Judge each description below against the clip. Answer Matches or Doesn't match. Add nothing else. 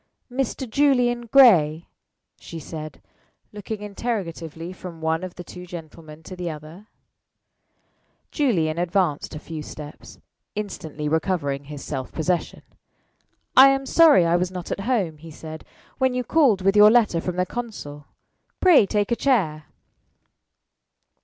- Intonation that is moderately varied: Doesn't match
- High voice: Doesn't match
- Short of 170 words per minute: Matches